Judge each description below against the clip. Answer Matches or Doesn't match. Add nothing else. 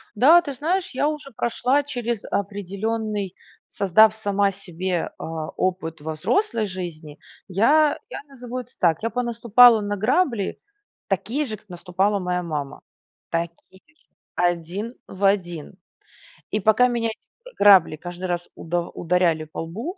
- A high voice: Matches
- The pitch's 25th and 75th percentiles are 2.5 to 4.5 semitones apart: Doesn't match